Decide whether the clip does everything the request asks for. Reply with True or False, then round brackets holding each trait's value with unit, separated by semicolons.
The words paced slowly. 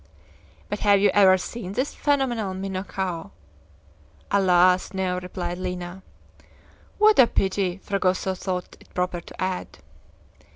True (120 wpm)